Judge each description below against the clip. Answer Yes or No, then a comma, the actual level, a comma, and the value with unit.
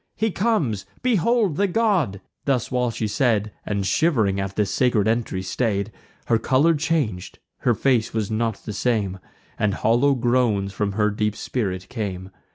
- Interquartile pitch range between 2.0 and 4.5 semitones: No, average, 5.2 semitones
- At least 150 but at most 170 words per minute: Yes, average, 160 wpm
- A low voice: Yes, low, 115 Hz